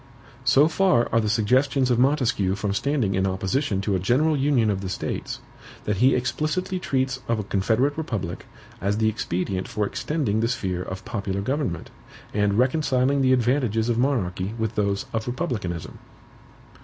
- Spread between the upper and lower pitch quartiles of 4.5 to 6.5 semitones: Yes, average, 5.2 semitones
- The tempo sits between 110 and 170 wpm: Yes, average, 165 wpm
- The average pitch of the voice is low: Yes, low, 115 Hz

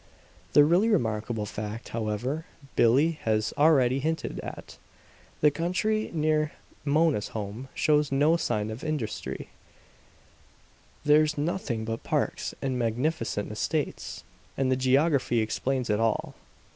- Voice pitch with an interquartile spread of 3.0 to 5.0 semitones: No, wide, 5.5 semitones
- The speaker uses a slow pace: Yes, slow, 120 wpm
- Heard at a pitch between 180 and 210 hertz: No, low, 135 Hz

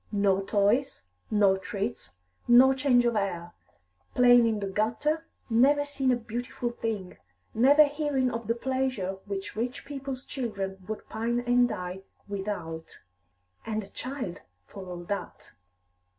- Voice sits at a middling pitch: No, high, 230 Hz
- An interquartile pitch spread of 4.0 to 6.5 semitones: Yes, average, 4.6 semitones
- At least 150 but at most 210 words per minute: No, slow, 135 wpm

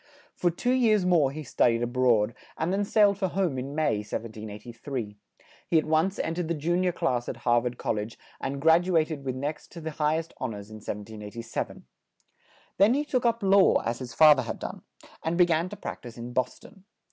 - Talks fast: Yes, fast, 230 wpm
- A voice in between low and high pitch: Yes, medium, 150 Hz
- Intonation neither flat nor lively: No, wide, 6.9 semitones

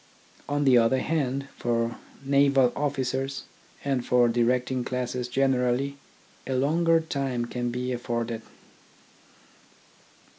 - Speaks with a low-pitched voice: Yes, low, 130 Hz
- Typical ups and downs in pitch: No, narrow, 2.1 semitones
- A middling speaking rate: No, slow, 105 wpm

